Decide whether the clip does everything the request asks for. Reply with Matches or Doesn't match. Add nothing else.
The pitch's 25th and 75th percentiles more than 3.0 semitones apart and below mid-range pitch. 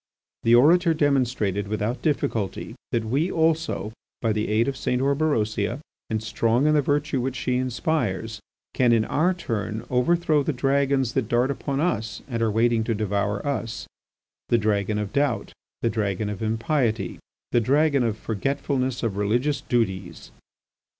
Matches